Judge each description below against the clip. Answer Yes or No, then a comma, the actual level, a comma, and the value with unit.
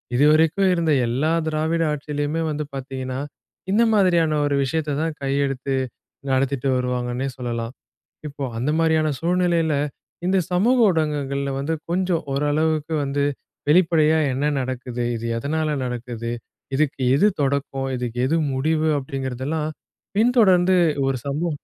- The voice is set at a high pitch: No, medium, 150 Hz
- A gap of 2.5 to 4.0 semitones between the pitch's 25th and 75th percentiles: Yes, average, 3.3 semitones